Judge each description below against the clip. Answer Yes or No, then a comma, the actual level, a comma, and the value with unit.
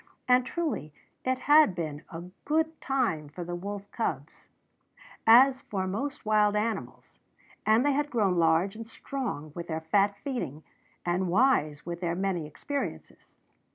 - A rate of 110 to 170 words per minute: Yes, average, 150 wpm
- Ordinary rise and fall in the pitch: No, wide, 7.2 semitones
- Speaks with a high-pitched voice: Yes, high, 205 Hz